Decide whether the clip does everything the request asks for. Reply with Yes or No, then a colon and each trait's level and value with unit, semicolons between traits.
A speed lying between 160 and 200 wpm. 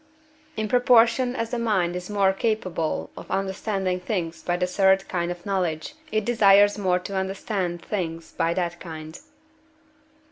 No: average, 150 wpm